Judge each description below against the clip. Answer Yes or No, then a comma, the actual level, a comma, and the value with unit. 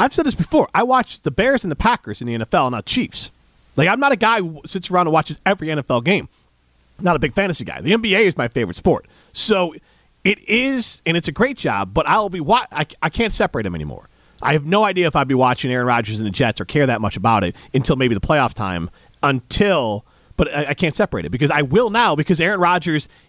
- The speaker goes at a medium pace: No, fast, 245 wpm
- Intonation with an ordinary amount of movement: No, wide, 8.6 semitones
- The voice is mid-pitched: Yes, medium, 155 Hz